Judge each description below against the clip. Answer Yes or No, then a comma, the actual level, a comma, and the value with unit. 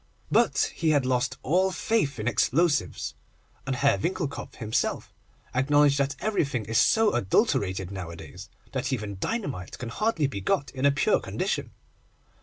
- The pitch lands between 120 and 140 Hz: Yes, low, 135 Hz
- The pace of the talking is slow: No, average, 145 wpm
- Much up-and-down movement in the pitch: Yes, wide, 6.5 semitones